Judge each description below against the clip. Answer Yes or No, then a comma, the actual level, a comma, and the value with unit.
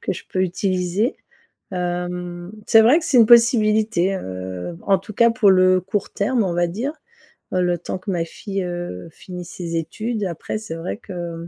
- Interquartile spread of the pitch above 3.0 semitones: Yes, average, 3.5 semitones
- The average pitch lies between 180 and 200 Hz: Yes, medium, 185 Hz